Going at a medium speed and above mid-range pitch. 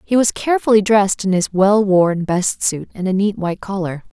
No: fast, 215 wpm; high, 200 Hz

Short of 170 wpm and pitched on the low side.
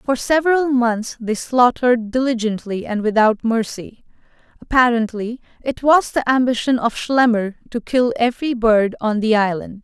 No: average, 140 wpm; high, 235 Hz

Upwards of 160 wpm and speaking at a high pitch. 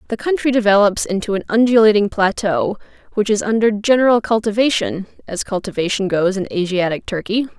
No: average, 140 wpm; high, 210 Hz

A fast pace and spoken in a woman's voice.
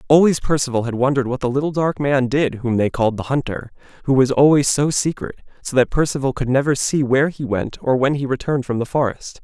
No: fast, 230 wpm; male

